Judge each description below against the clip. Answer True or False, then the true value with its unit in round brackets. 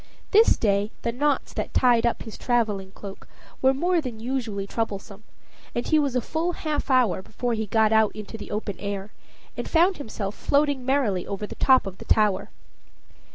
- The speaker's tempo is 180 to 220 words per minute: True (185 wpm)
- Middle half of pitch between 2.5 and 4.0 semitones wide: False (4.6 semitones)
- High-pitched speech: True (230 Hz)